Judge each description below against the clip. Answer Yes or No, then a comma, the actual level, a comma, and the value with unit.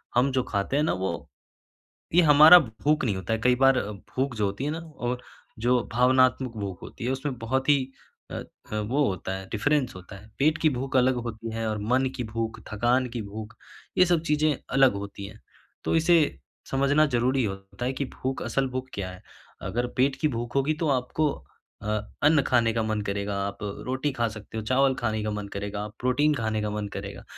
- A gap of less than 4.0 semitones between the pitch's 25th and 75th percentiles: No, average, 4.3 semitones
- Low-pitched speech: Yes, low, 125 Hz